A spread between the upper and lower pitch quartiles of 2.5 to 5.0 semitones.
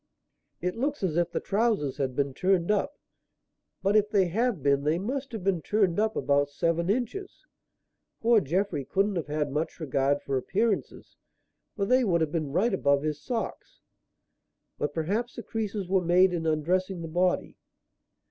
No: wide, 5.4 semitones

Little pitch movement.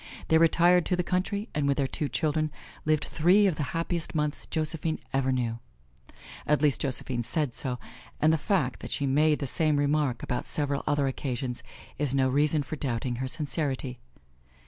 No: average, 3.1 semitones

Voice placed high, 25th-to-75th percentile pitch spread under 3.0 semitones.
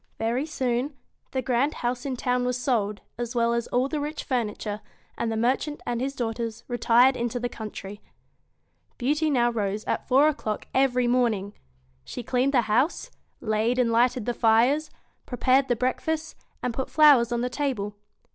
Yes: high, 245 Hz; narrow, 2.4 semitones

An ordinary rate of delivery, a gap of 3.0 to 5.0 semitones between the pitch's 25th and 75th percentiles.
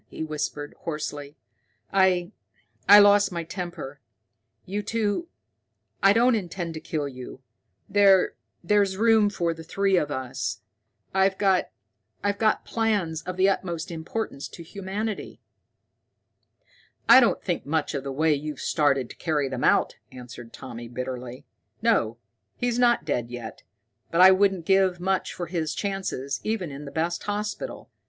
No: average, 145 wpm; wide, 5.4 semitones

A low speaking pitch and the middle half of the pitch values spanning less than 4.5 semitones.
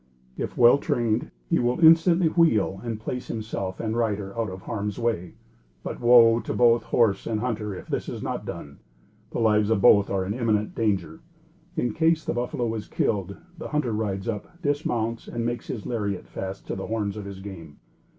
Yes: low, 110 Hz; average, 3.2 semitones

